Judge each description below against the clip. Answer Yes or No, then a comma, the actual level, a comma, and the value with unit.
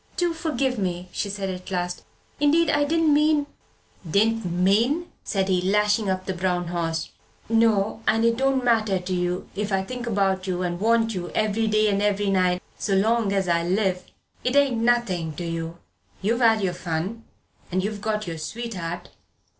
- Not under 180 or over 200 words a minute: Yes, average, 185 wpm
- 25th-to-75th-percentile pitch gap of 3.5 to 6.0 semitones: Yes, average, 4.1 semitones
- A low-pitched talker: No, high, 200 Hz